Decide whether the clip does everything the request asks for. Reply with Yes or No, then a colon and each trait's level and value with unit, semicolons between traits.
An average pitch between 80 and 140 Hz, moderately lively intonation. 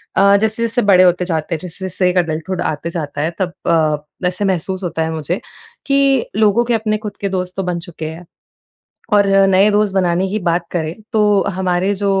No: medium, 185 Hz; average, 3.0 semitones